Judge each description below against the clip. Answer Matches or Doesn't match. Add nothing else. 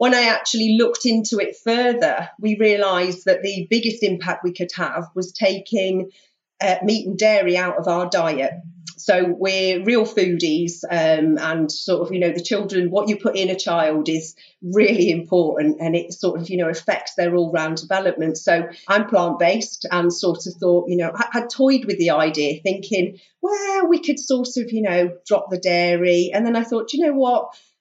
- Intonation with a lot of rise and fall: Doesn't match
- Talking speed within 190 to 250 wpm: Matches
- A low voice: Doesn't match